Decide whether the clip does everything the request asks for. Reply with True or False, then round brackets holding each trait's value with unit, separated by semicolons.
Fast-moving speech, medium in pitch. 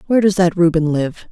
True (230 wpm; 175 Hz)